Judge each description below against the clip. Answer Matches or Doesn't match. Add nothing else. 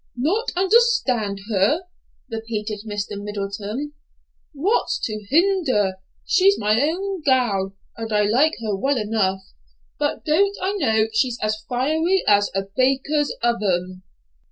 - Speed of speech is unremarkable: Doesn't match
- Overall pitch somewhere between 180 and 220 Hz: Doesn't match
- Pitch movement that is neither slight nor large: Doesn't match